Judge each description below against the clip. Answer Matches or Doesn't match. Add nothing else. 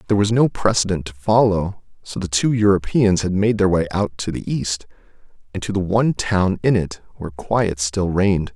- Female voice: Doesn't match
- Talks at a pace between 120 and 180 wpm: Doesn't match